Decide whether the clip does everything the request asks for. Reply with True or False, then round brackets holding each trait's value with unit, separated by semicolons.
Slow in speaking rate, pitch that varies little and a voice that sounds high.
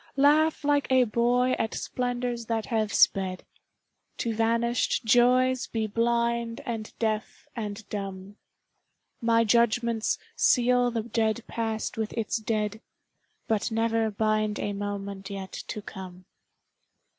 True (120 wpm; 2.0 semitones; 225 Hz)